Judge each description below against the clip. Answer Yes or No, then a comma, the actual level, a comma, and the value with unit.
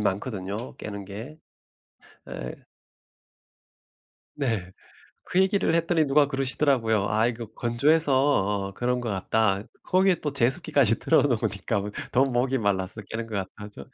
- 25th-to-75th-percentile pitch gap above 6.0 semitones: No, average, 5.3 semitones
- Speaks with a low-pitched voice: Yes, low, 115 Hz